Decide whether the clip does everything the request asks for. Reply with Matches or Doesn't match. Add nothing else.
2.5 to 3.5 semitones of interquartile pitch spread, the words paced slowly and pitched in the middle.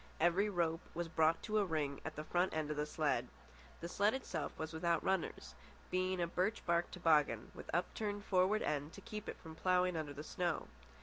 Doesn't match